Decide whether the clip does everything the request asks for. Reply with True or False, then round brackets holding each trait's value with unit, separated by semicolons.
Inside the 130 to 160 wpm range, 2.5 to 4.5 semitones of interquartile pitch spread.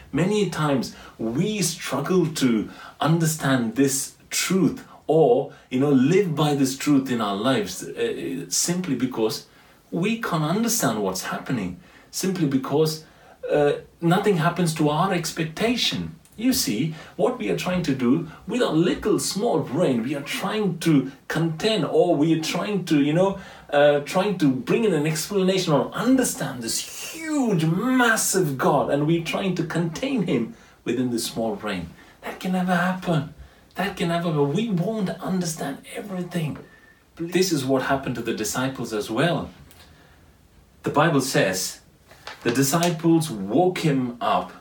False (150 wpm; 5.2 semitones)